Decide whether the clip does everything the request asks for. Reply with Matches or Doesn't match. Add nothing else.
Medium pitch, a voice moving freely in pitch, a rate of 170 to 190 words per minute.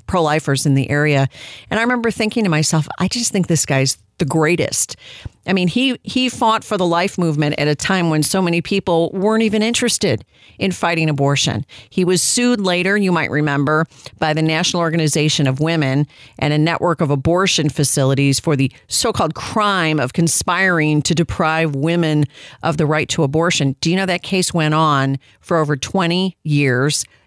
Doesn't match